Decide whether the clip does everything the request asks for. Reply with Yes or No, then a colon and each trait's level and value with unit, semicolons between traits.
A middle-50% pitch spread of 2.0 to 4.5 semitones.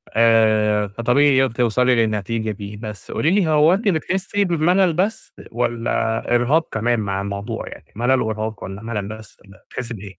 No: wide, 5.4 semitones